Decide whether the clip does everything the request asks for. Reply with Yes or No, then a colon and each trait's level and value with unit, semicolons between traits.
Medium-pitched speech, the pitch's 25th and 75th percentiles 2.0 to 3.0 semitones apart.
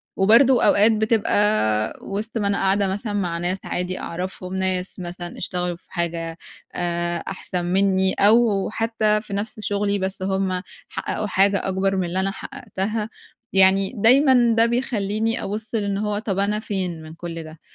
No: high, 195 Hz; average, 2.7 semitones